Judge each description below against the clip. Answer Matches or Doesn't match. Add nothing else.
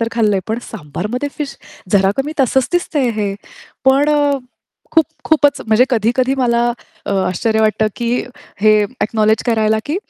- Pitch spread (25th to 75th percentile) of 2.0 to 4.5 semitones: Matches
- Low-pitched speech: Doesn't match